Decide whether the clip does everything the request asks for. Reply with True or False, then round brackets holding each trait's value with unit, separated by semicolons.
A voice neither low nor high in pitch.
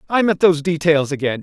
True (165 Hz)